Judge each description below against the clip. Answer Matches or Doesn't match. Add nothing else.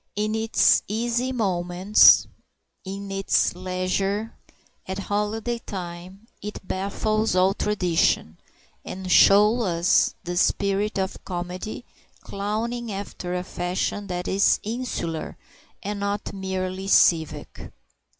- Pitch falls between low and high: Doesn't match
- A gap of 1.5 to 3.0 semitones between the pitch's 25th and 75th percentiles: Matches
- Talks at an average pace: Doesn't match